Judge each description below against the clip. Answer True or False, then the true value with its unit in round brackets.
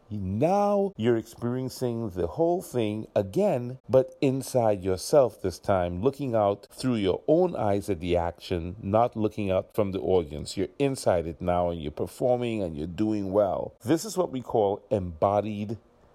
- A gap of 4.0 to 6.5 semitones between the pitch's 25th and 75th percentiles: True (4.7 semitones)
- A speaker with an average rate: True (165 wpm)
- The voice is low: True (110 Hz)